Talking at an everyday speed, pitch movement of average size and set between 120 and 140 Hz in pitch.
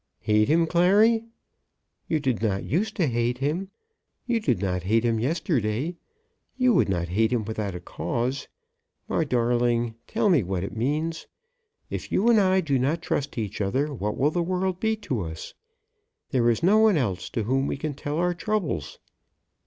No: average, 180 wpm; wide, 8.0 semitones; low, 135 Hz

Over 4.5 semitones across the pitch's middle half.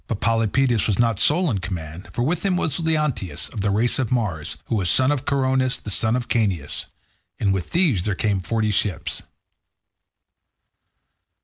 Yes: average, 5.1 semitones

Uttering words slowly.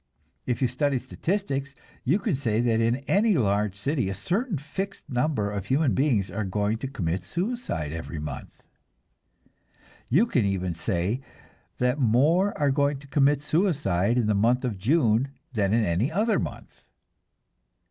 No: average, 155 wpm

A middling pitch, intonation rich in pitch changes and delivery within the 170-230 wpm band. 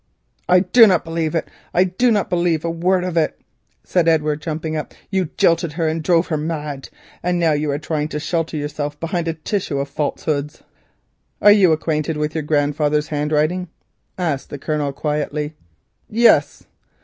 No: medium, 160 Hz; narrow, 2.6 semitones; average, 175 wpm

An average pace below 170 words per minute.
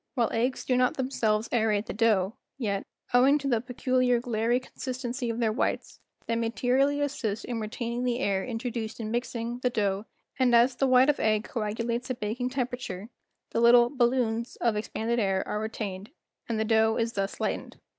No: average, 185 wpm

